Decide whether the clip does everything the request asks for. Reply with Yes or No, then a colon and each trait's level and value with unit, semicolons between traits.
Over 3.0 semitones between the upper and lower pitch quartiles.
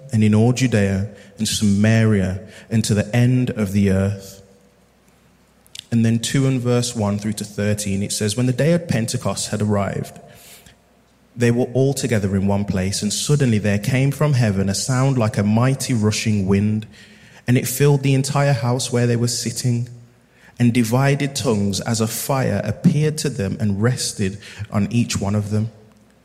Yes: average, 3.6 semitones